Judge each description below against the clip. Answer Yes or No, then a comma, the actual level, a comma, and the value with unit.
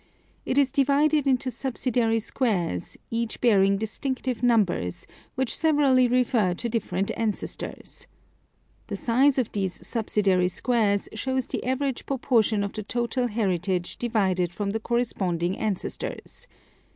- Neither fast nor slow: No, slow, 125 wpm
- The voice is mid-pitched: No, high, 230 Hz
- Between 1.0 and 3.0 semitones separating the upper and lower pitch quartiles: No, average, 4.5 semitones